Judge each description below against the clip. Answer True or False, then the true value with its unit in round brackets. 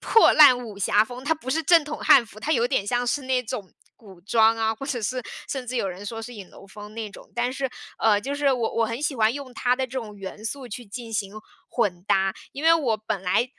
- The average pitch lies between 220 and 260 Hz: True (235 Hz)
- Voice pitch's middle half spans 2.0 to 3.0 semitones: False (3.8 semitones)